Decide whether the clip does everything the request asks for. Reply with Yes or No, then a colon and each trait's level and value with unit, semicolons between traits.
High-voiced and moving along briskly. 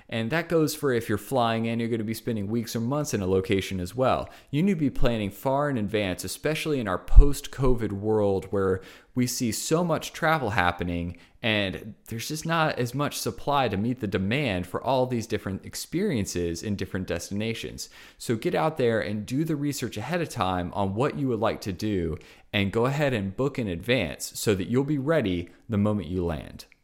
No: low, 115 Hz; fast, 210 wpm